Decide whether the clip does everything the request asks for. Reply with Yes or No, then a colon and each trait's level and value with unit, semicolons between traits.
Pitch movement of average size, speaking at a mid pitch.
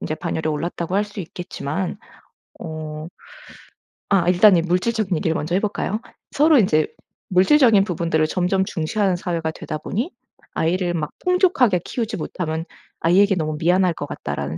Yes: average, 3.9 semitones; medium, 180 Hz